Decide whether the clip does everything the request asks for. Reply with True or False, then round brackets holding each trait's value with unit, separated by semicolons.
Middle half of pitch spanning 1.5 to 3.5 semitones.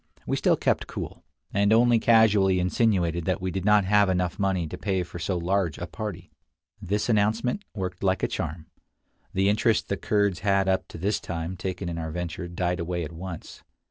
True (2.8 semitones)